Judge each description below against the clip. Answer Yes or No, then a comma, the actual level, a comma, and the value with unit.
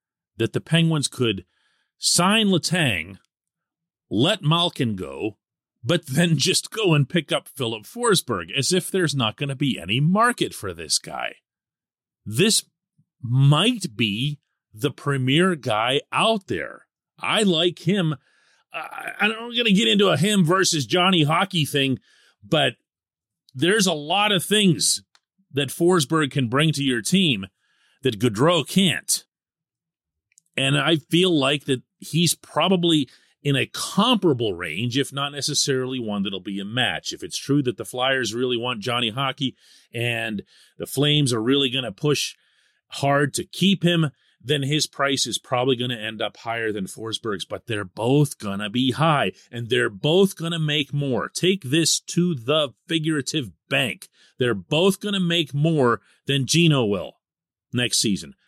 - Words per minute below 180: Yes, average, 155 wpm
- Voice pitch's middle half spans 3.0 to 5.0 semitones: No, wide, 5.6 semitones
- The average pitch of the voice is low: No, medium, 145 Hz